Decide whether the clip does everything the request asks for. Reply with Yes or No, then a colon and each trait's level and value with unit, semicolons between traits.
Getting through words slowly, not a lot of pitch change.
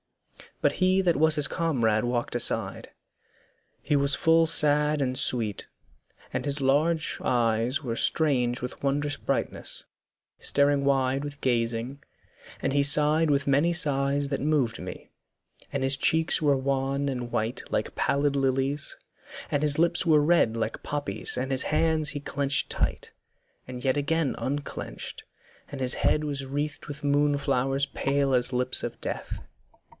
No: average, 150 wpm; narrow, 2.2 semitones